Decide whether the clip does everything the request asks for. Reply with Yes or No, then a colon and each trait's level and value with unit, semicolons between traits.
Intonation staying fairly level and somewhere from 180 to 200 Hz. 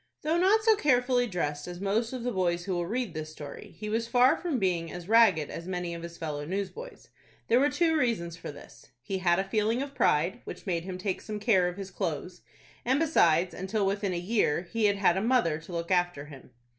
No: wide, 5.5 semitones; high, 190 Hz